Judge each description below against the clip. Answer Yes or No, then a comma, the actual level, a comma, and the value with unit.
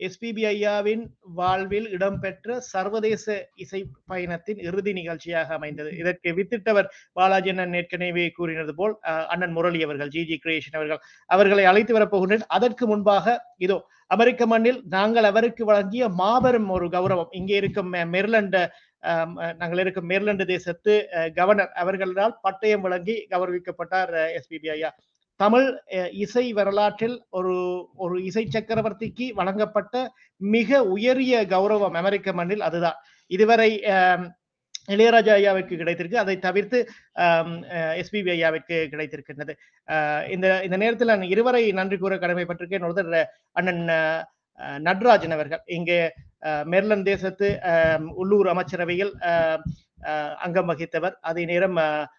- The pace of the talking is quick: No, average, 110 wpm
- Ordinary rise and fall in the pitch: Yes, average, 3.5 semitones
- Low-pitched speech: No, medium, 185 Hz